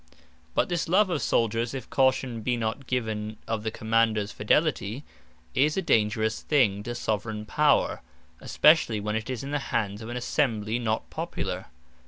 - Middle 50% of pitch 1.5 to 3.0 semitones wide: No, average, 3.7 semitones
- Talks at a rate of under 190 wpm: Yes, average, 165 wpm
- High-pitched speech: No, low, 115 Hz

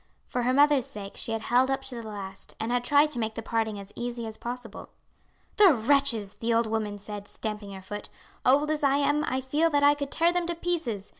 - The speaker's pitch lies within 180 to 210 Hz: No, high, 245 Hz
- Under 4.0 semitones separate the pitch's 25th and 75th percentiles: No, average, 4.8 semitones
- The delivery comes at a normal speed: No, fast, 235 wpm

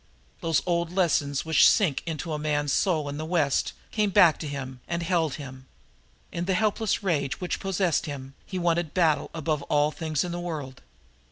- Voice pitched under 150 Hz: No, medium, 160 Hz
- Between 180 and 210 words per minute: Yes, average, 185 wpm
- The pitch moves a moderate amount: Yes, average, 3.3 semitones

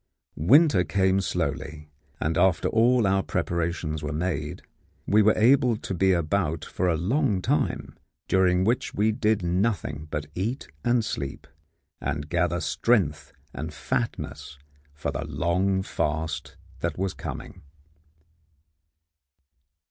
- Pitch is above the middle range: No, very low, 90 Hz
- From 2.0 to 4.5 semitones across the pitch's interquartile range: No, average, 5.0 semitones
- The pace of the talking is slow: Yes, slow, 125 wpm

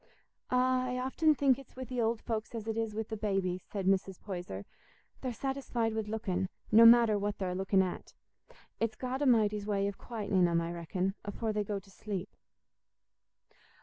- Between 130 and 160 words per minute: No, average, 180 wpm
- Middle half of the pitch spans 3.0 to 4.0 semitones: Yes, average, 3.5 semitones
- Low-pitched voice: No, high, 215 Hz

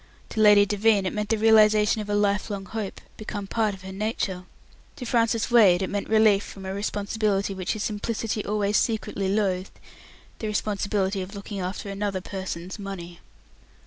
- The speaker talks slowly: No, average, 170 wpm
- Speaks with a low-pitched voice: No, high, 205 Hz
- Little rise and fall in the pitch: Yes, narrow, 1.7 semitones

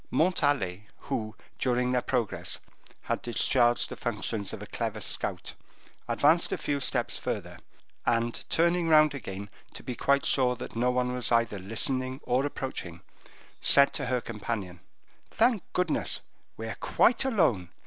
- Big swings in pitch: No, average, 4.1 semitones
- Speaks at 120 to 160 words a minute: Yes, average, 150 wpm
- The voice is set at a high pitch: No, low, 125 Hz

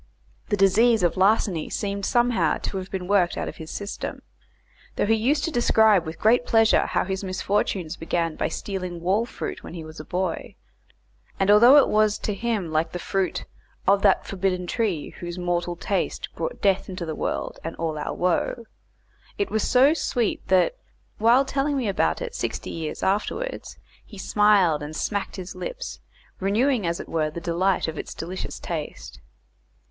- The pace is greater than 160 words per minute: Yes, average, 180 wpm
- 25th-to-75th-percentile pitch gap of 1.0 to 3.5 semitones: No, average, 4.3 semitones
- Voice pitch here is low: No, high, 195 Hz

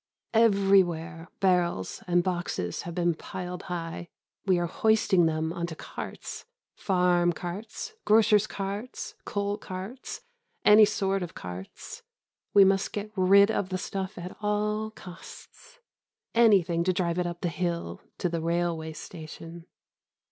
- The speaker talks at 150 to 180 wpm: No, slow, 135 wpm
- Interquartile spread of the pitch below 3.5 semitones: Yes, average, 2.8 semitones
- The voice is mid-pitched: Yes, medium, 180 Hz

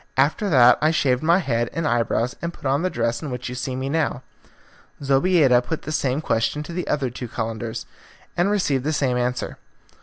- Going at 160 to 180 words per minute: No, fast, 205 wpm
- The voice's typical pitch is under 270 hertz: Yes, low, 135 Hz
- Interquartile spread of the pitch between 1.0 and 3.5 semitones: No, average, 4.2 semitones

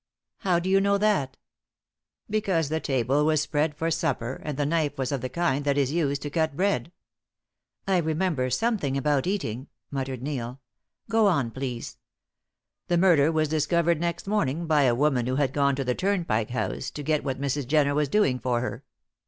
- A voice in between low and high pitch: Yes, medium, 145 Hz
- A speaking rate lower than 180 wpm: No, average, 185 wpm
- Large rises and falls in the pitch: No, average, 4.2 semitones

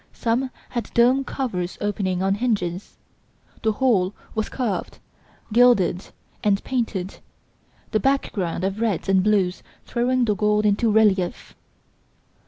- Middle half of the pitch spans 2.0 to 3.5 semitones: No, average, 3.9 semitones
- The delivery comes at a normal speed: No, slow, 120 wpm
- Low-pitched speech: No, high, 210 Hz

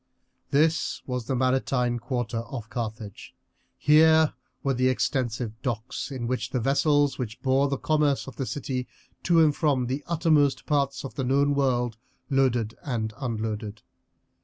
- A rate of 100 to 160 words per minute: Yes, average, 150 wpm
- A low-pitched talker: Yes, low, 130 Hz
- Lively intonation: No, average, 3.0 semitones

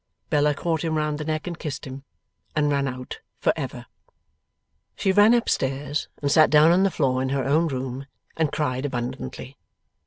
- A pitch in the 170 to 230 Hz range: No, medium, 145 Hz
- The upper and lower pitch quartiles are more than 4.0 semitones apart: No, average, 2.8 semitones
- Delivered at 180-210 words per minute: Yes, average, 185 wpm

